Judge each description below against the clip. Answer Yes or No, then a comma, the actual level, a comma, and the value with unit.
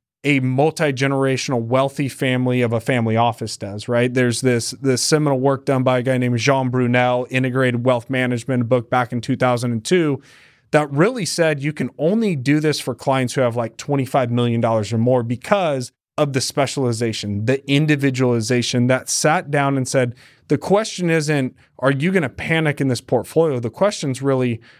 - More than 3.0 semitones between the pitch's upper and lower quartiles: No, narrow, 2.5 semitones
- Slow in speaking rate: No, average, 175 wpm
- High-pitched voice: No, low, 130 Hz